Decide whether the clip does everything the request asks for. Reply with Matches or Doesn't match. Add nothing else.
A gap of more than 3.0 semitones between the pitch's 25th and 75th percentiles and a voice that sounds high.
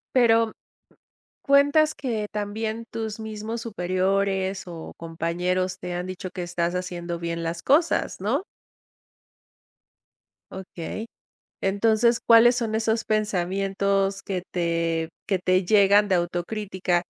Matches